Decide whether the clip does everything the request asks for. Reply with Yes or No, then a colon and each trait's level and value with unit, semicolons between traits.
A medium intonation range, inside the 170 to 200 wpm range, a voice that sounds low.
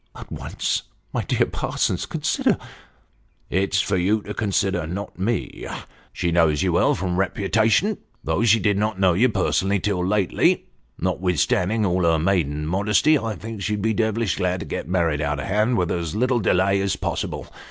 Yes: average, 3.3 semitones; average, 175 wpm; very low, 95 Hz